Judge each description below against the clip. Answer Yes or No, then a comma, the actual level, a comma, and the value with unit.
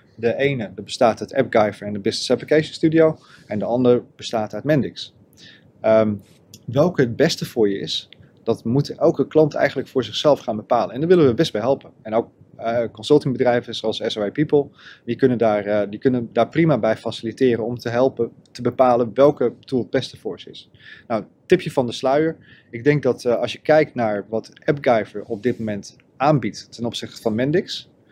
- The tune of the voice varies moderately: Yes, average, 4.3 semitones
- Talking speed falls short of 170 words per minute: No, average, 195 wpm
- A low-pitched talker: Yes, low, 120 Hz